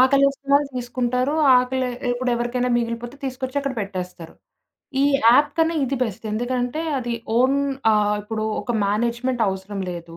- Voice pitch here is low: No, high, 245 Hz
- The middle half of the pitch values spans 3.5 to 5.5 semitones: No, average, 2.9 semitones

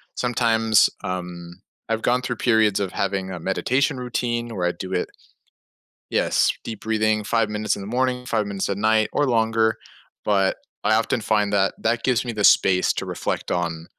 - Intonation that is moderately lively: Yes, average, 3.2 semitones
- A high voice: No, low, 110 Hz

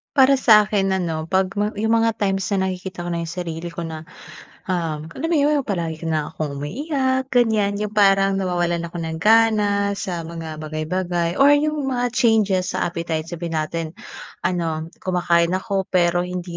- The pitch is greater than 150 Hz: Yes, medium, 185 Hz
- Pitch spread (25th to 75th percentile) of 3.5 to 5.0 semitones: Yes, average, 4.2 semitones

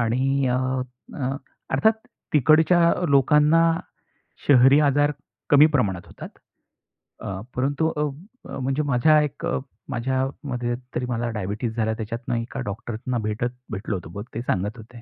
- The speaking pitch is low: Yes, low, 125 Hz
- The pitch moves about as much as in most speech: Yes, average, 4.0 semitones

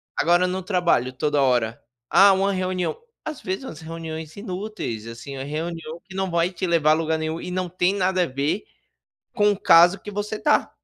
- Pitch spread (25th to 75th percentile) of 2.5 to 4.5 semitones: Yes, average, 3.3 semitones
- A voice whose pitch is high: No, medium, 175 Hz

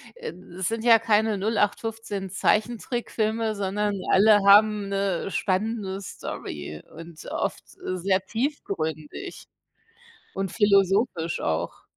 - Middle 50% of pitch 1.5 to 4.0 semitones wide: Yes, average, 2.7 semitones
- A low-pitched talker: No, high, 200 Hz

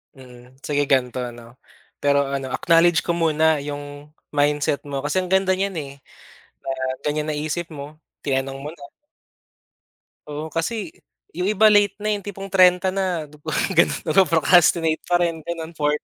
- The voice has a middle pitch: Yes, medium, 155 Hz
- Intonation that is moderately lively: Yes, average, 3.6 semitones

